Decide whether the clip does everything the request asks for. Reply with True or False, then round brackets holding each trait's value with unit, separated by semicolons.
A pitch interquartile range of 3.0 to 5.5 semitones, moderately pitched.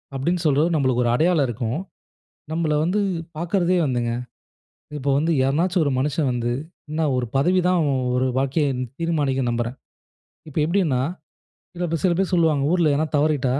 True (4.4 semitones; 150 Hz)